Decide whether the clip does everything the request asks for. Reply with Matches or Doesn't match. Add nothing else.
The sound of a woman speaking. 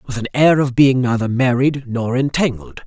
Doesn't match